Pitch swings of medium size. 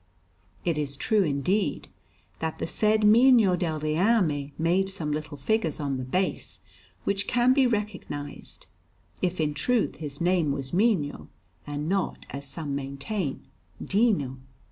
No: wide, 6.3 semitones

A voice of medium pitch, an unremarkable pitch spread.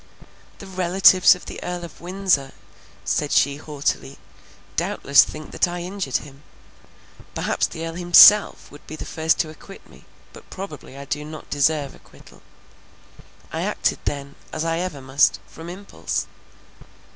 Yes: medium, 160 Hz; average, 3.8 semitones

